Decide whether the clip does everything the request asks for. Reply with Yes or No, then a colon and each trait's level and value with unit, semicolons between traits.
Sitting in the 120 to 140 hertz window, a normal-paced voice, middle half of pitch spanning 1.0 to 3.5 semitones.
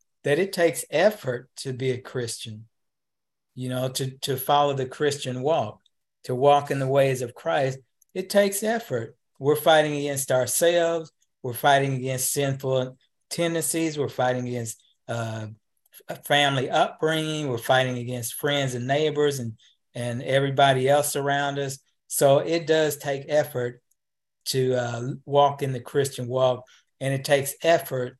Yes: low, 135 Hz; average, 150 wpm; narrow, 2.4 semitones